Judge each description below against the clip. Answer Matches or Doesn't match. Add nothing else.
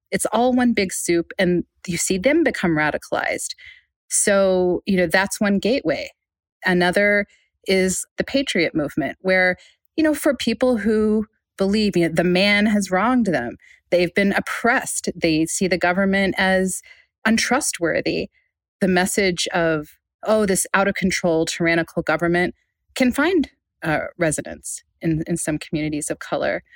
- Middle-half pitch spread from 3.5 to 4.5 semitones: Matches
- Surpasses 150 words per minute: Doesn't match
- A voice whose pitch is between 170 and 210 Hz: Matches